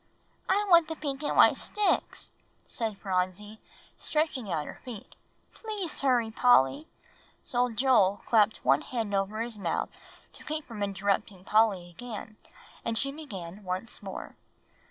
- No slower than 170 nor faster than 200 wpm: No, average, 140 wpm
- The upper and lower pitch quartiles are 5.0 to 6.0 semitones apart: Yes, wide, 5.6 semitones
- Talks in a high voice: Yes, high, 220 Hz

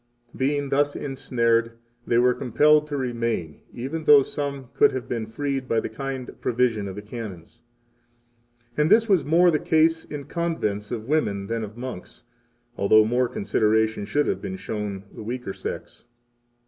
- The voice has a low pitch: Yes, low, 125 Hz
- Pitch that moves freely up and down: No, average, 4.8 semitones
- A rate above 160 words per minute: Yes, average, 170 wpm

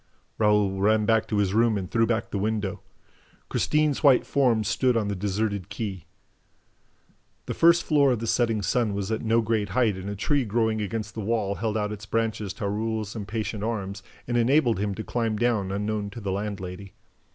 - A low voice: Yes, low, 110 Hz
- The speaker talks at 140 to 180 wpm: No, average, 195 wpm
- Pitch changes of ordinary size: No, narrow, 2.2 semitones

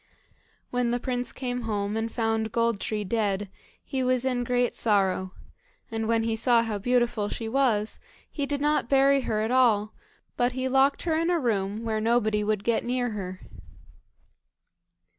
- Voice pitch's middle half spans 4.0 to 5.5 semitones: No, average, 2.8 semitones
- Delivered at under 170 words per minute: No, average, 175 wpm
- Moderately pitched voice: No, high, 230 Hz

